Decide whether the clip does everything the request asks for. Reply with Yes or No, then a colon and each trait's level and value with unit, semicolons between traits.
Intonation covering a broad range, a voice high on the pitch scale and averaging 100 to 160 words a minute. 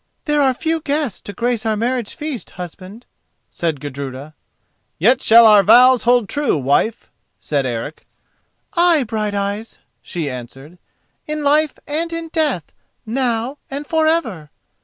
Yes: wide, 8.5 semitones; high, 230 Hz; slow, 135 wpm